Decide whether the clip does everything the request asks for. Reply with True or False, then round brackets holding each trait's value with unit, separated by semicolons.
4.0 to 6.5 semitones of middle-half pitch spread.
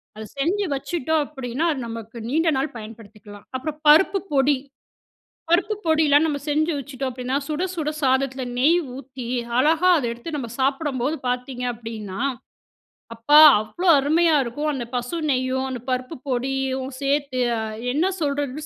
False (3.5 semitones)